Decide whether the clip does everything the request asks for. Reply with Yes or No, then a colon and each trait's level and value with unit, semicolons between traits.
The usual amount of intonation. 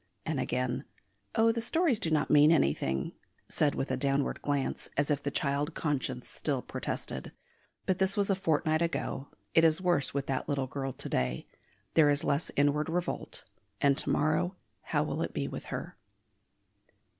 Yes: average, 3.2 semitones